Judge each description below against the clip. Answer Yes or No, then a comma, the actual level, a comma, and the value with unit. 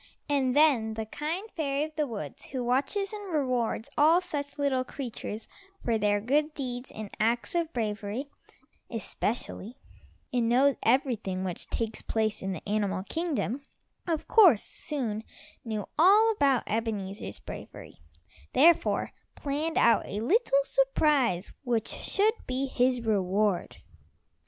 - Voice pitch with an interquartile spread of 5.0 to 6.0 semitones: Yes, wide, 5.5 semitones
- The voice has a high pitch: Yes, very high, 250 Hz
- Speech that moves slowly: Yes, slow, 130 wpm